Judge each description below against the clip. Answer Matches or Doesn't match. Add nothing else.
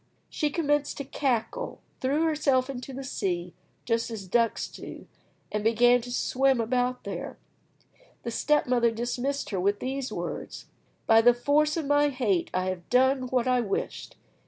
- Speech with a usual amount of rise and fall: Matches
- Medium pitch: Doesn't match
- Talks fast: Doesn't match